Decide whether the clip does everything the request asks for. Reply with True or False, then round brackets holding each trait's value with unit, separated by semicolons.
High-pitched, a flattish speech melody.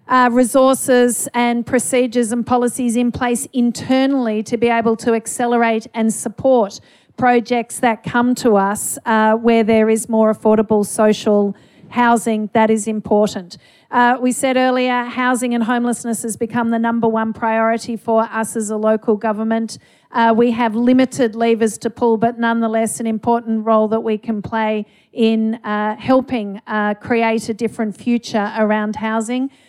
True (230 Hz; 1.7 semitones)